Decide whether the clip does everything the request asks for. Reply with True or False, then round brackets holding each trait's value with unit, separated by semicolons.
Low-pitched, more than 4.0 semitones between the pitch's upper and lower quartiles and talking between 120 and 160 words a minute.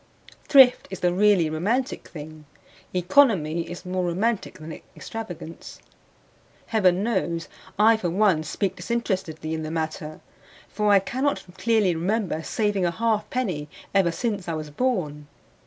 False (185 Hz; 5.1 semitones; 140 wpm)